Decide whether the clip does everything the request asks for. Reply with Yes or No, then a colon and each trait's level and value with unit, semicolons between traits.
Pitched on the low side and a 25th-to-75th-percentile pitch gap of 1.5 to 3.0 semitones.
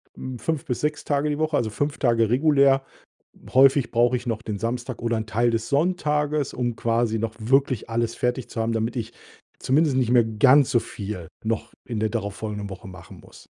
No: low, 120 Hz; average, 3.6 semitones